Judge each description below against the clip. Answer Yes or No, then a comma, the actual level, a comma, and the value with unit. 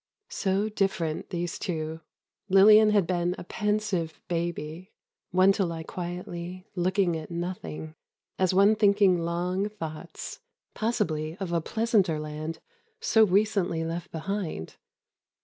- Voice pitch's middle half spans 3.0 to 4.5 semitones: Yes, average, 3.3 semitones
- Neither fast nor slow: No, slow, 115 wpm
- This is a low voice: No, medium, 180 Hz